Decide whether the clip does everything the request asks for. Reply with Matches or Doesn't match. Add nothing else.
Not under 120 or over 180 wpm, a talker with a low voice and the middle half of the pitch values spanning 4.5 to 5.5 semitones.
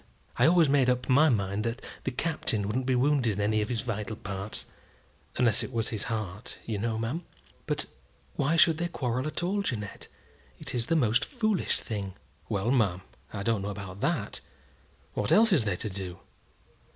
Doesn't match